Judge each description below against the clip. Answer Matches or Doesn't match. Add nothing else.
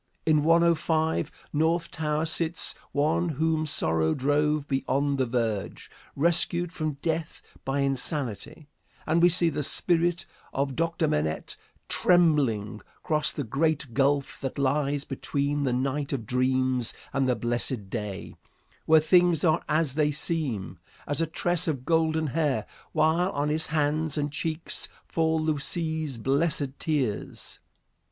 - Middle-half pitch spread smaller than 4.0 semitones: Matches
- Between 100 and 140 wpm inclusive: Matches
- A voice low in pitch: Doesn't match